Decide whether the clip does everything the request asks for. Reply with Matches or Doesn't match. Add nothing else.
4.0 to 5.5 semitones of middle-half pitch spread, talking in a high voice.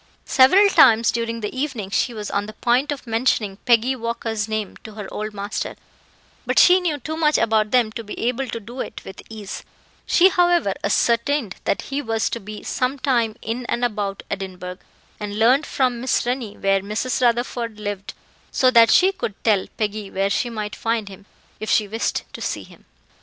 Doesn't match